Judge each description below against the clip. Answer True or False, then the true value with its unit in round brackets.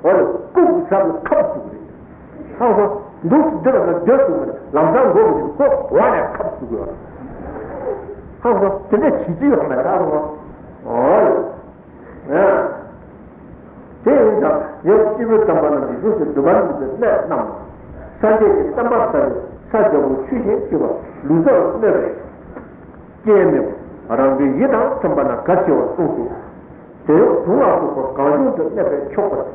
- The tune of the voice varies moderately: False (8.6 semitones)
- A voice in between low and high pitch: False (220 Hz)